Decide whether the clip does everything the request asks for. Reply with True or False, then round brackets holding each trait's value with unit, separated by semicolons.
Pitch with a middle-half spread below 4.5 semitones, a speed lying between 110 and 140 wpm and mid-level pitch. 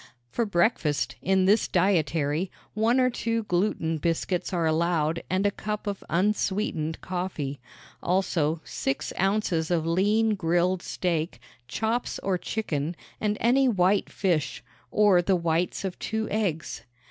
True (4.1 semitones; 135 wpm; 180 Hz)